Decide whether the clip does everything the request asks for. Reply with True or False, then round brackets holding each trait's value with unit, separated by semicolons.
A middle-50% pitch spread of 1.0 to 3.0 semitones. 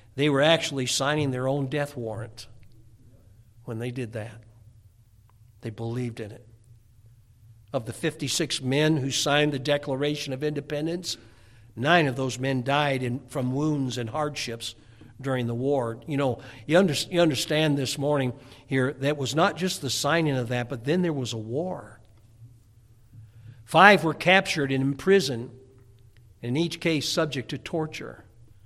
False (4.4 semitones)